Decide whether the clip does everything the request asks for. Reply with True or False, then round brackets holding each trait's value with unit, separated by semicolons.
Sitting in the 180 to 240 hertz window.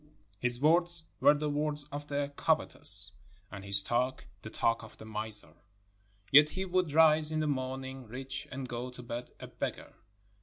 False (130 Hz)